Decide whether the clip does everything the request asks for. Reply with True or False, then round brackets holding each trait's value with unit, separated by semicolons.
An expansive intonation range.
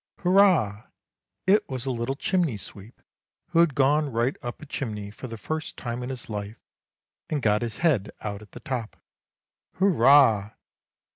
True (6.0 semitones)